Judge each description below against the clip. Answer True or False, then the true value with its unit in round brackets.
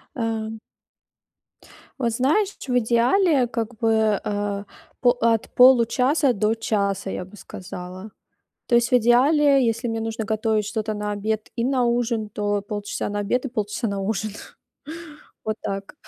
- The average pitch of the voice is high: True (225 Hz)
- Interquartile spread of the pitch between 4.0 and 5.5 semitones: False (2.8 semitones)